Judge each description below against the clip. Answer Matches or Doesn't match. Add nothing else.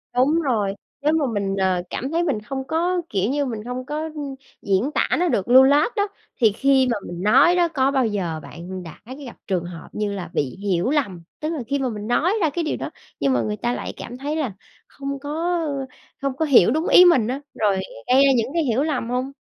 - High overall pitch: Matches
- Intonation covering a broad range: Matches